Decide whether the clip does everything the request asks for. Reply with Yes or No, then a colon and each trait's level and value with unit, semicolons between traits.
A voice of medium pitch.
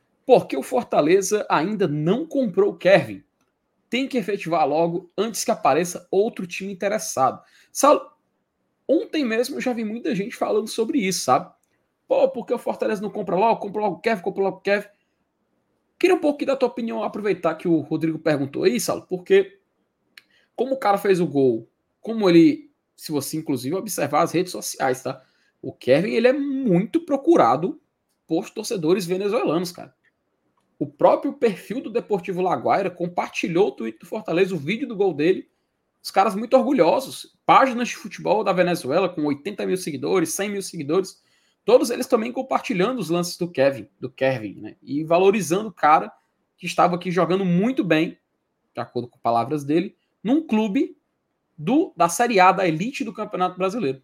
No: high, 200 Hz